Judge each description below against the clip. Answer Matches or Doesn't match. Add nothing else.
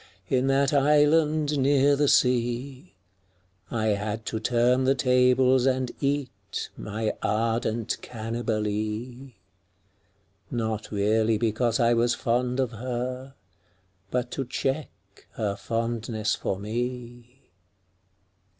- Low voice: Matches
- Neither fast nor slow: Doesn't match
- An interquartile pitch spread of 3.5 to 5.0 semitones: Doesn't match